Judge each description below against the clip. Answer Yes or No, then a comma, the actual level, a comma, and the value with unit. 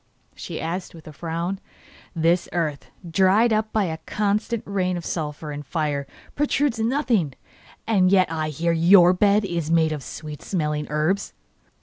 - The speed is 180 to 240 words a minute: No, average, 155 wpm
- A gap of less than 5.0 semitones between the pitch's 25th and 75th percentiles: Yes, average, 4.2 semitones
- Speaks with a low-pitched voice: No, medium, 175 Hz